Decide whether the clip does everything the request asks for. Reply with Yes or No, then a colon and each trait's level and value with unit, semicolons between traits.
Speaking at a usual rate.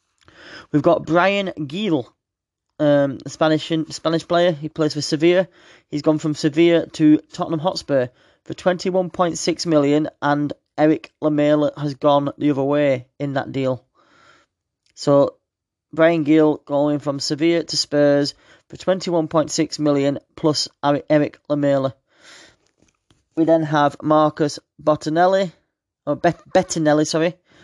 No: slow, 120 wpm